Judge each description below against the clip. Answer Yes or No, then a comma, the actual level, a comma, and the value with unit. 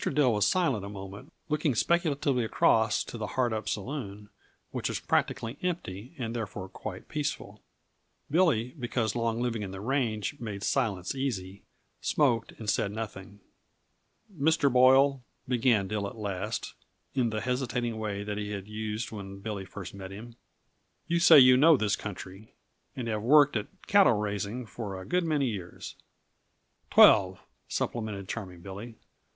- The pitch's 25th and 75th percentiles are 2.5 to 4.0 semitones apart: No, average, 4.4 semitones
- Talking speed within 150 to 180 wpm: Yes, average, 155 wpm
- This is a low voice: Yes, low, 110 Hz